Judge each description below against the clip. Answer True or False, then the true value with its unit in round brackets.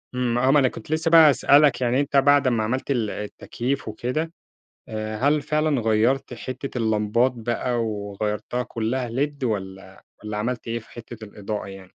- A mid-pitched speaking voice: False (120 Hz)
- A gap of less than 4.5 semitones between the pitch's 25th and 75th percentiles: True (4.0 semitones)